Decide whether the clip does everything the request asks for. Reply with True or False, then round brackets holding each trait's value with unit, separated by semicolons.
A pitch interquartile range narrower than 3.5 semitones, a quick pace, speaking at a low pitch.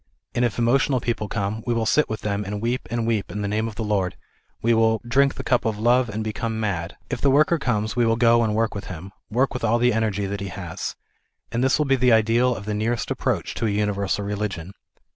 True (2.6 semitones; 255 wpm; 110 Hz)